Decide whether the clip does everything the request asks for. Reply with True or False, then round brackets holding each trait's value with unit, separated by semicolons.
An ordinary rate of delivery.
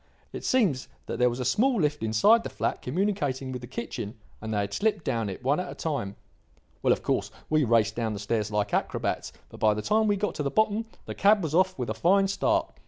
False (240 wpm)